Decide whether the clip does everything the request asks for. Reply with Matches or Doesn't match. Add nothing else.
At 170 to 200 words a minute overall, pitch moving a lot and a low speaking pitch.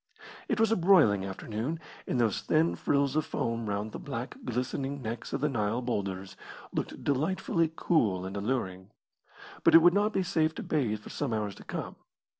Matches